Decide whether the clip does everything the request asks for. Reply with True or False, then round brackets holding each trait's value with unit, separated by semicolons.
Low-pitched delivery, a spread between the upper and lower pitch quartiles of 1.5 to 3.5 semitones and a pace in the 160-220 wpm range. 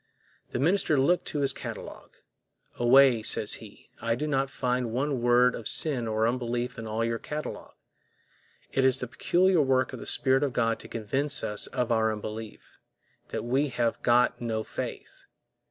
True (125 Hz; 2.9 semitones; 170 wpm)